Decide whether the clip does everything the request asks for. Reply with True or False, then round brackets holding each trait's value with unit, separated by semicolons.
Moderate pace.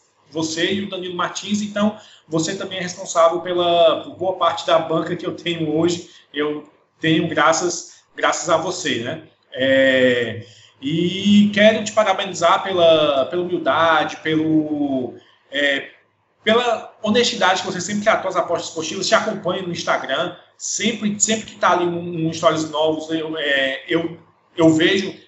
True (150 wpm)